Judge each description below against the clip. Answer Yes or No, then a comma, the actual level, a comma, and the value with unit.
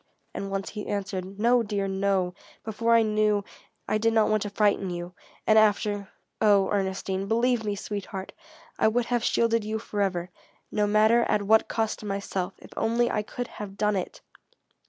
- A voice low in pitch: No, high, 210 Hz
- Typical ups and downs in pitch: No, narrow, 2.0 semitones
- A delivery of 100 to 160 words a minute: No, average, 175 wpm